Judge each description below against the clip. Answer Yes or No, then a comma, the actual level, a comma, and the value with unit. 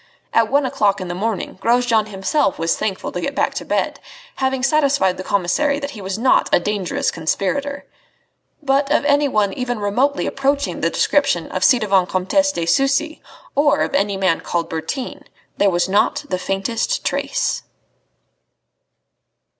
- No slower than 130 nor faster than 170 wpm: Yes, average, 160 wpm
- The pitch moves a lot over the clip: Yes, wide, 6.7 semitones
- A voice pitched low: No, high, 225 Hz